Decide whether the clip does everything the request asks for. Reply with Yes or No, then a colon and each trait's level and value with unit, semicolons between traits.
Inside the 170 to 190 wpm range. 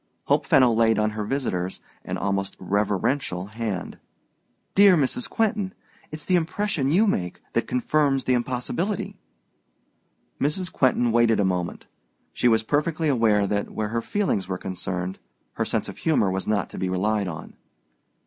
No: average, 155 wpm